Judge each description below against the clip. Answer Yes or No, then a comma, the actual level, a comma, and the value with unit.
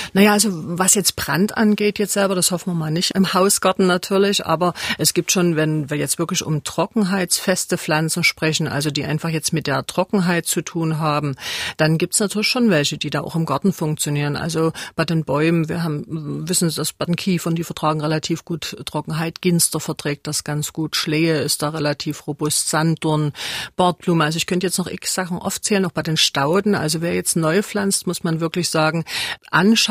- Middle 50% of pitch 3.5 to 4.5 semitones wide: No, average, 3.1 semitones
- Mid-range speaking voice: Yes, medium, 165 Hz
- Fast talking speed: Yes, fast, 205 wpm